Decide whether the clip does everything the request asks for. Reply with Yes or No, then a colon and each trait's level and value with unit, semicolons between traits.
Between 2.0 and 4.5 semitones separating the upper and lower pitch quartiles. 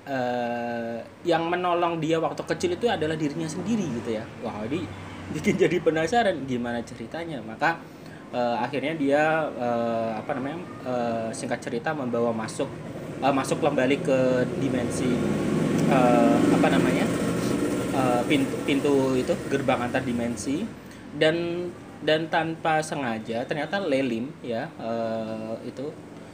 No: average, 5.2 semitones